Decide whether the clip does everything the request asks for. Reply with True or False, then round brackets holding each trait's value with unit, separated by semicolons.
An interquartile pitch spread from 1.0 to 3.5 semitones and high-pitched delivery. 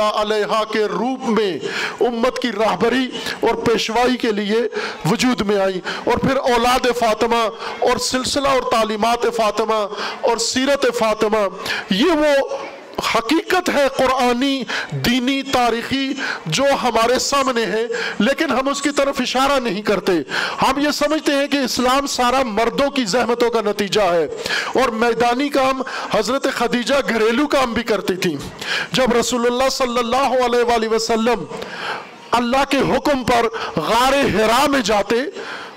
True (3.1 semitones; 245 Hz)